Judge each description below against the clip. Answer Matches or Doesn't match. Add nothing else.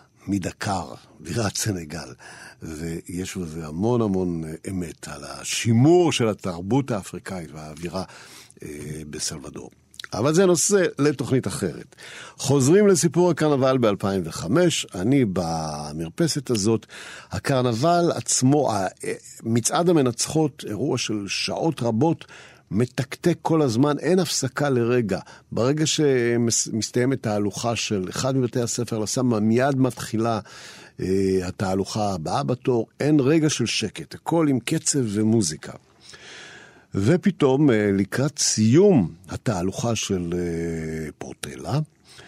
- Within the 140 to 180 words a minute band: Doesn't match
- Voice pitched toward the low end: Matches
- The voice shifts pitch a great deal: Matches